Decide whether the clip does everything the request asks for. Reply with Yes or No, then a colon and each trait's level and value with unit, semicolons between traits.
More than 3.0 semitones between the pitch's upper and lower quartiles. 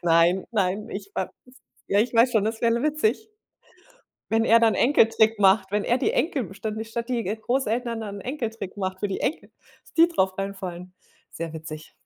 Yes: average, 3.6 semitones